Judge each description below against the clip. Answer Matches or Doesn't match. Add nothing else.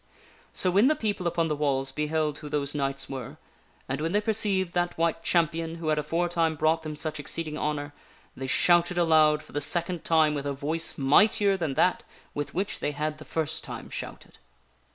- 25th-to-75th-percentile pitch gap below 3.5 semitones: Matches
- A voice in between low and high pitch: Matches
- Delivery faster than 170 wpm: Matches